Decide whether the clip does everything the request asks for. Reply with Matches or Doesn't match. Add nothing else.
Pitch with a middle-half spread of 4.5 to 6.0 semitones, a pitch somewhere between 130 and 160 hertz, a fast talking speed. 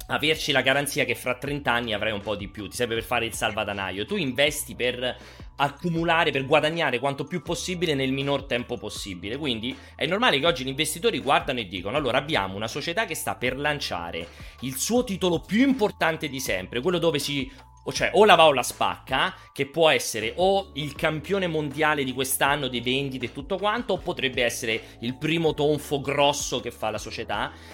Matches